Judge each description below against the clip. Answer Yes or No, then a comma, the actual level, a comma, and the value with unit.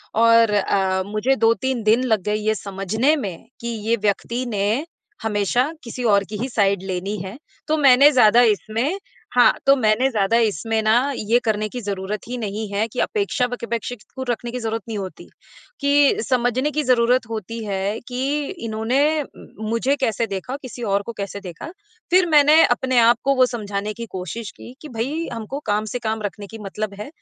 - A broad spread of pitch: No, average, 3.4 semitones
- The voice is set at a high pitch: Yes, high, 225 Hz